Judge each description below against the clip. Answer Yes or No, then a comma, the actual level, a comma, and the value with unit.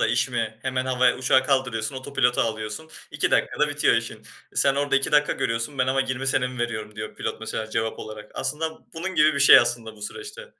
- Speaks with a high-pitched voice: No, low, 130 Hz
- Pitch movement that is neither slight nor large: Yes, average, 3.7 semitones